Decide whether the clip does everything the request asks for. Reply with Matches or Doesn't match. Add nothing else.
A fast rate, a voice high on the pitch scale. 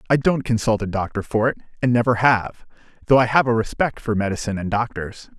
Doesn't match